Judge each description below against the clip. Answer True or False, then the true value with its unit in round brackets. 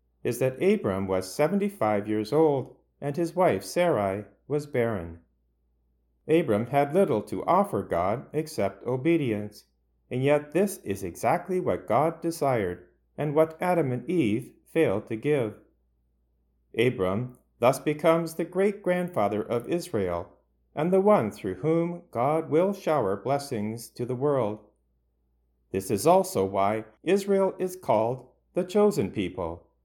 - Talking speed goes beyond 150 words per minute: False (135 wpm)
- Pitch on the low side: True (125 Hz)